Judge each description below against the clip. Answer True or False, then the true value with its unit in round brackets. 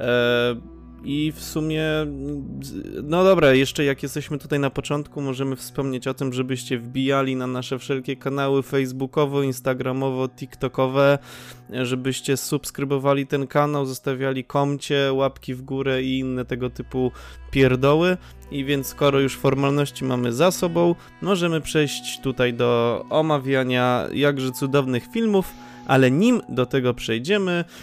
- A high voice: False (135 Hz)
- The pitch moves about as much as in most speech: False (2.1 semitones)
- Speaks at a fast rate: False (125 wpm)